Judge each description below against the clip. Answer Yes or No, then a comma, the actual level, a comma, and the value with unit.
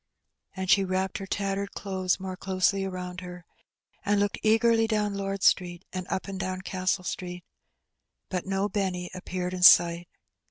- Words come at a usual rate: Yes, average, 160 wpm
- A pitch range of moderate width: No, narrow, 1.5 semitones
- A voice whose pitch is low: No, high, 190 Hz